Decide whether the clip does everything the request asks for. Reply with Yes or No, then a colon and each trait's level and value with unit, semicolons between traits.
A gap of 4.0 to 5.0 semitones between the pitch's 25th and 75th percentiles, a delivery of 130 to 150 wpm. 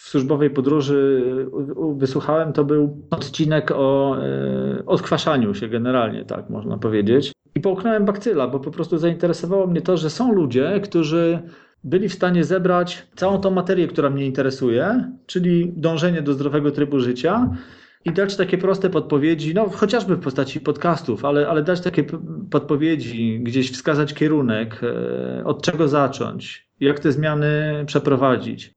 Yes: average, 4.3 semitones; average, 140 wpm